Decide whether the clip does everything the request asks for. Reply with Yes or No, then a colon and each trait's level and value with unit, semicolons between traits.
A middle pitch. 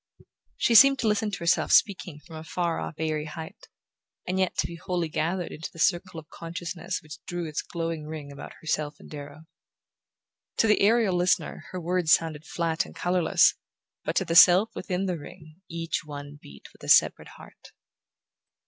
Yes: medium, 170 Hz